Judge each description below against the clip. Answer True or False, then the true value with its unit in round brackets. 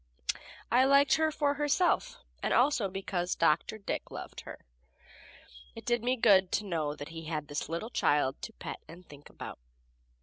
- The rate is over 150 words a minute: True (170 wpm)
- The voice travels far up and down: True (8.1 semitones)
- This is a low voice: False (195 Hz)